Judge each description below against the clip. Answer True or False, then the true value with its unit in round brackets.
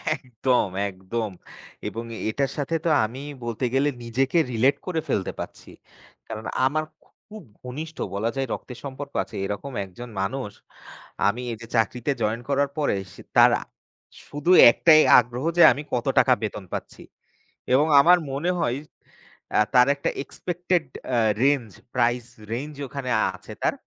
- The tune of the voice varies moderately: True (3.7 semitones)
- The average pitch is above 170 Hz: False (130 Hz)